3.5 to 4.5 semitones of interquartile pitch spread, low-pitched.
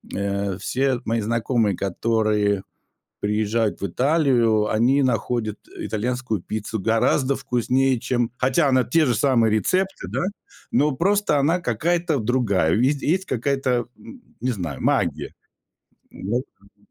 Yes: average, 4.0 semitones; low, 120 Hz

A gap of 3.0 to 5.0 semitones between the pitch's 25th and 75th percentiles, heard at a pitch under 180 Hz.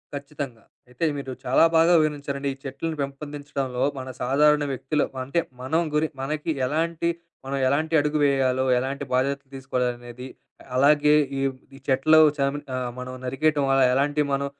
No: narrow, 2.4 semitones; medium, 140 Hz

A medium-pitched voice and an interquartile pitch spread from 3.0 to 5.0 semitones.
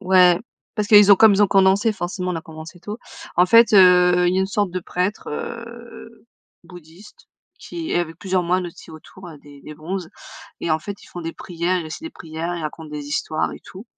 Yes: medium, 180 Hz; average, 3.5 semitones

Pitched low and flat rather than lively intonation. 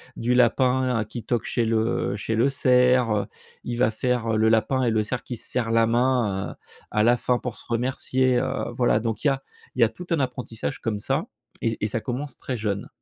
Yes: low, 120 Hz; narrow, 2.3 semitones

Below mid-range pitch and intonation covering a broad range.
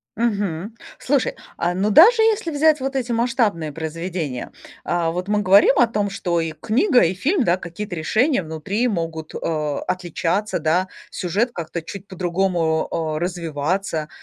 No: medium, 185 Hz; wide, 5.7 semitones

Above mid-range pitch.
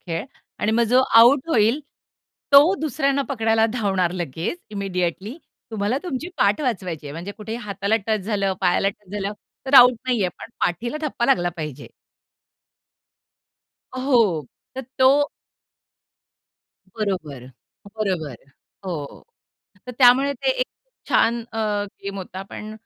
Yes: high, 215 Hz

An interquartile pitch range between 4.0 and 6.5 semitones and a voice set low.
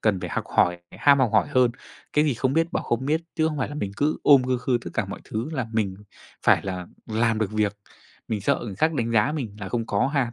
Yes: average, 5.0 semitones; low, 120 Hz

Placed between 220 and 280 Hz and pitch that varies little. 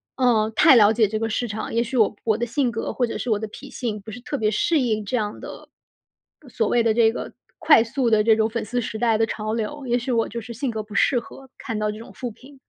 Yes: high, 225 Hz; narrow, 2.1 semitones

